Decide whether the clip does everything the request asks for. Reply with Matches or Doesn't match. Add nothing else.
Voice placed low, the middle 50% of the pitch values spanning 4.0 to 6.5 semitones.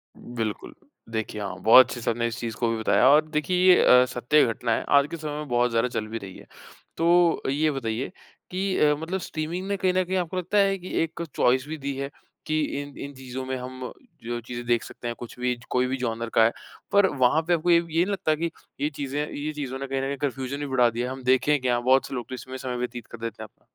Matches